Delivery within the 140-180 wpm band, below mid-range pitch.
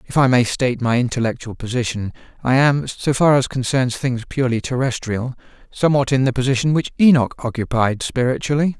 Yes: average, 165 wpm; low, 130 Hz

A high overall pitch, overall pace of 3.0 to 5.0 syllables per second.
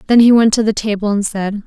No: high, 215 Hz; 6.1 syllables/s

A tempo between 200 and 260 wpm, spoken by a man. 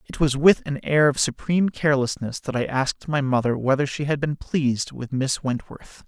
Yes: fast, 205 wpm; male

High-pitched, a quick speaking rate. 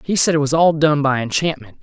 No: medium, 150 Hz; fast, 260 wpm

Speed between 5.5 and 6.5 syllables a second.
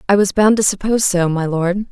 Yes: 5.8 syllables/s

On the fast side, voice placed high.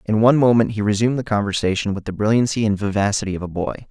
No: fast, 230 wpm; low, 105 Hz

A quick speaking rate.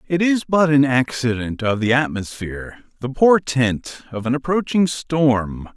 No: slow, 135 wpm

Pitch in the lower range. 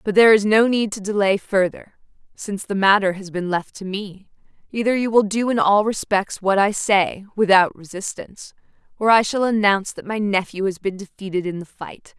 No: high, 200 Hz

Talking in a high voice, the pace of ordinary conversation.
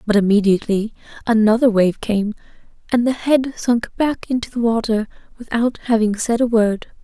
Yes: high, 225 Hz; average, 155 wpm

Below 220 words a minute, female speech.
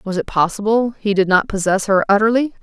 Yes: fast, 205 wpm; female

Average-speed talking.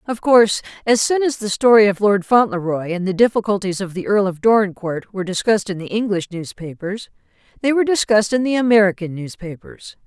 Yes: average, 185 wpm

